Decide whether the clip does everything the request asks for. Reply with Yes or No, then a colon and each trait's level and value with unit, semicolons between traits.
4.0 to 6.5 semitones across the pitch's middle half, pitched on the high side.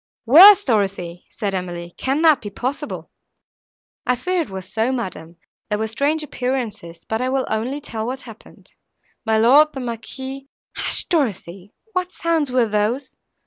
Yes: average, 5.1 semitones; high, 245 Hz